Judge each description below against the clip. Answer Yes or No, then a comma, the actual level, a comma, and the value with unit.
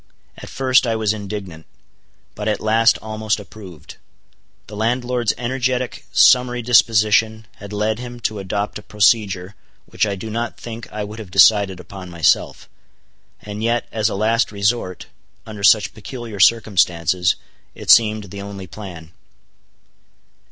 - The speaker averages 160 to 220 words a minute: No, average, 140 wpm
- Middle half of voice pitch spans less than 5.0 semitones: Yes, narrow, 2.5 semitones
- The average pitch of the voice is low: Yes, low, 105 Hz